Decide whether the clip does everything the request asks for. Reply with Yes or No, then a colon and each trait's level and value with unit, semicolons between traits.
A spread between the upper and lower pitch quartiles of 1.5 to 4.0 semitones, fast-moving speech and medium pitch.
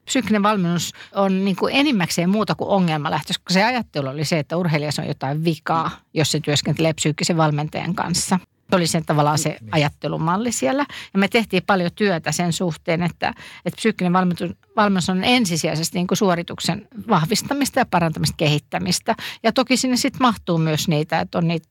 No: average, 4.4 semitones; fast, 170 wpm; medium, 175 Hz